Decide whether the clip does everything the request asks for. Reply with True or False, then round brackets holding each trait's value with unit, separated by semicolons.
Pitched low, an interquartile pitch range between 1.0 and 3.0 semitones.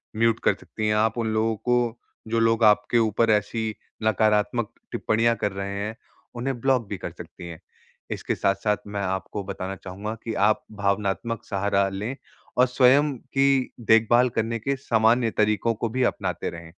True (110 Hz; 2.5 semitones)